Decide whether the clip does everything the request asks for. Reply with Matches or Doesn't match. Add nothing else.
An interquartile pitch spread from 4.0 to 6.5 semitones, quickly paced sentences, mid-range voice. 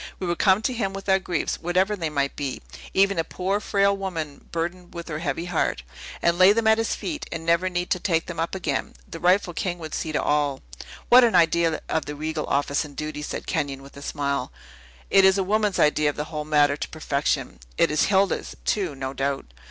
Matches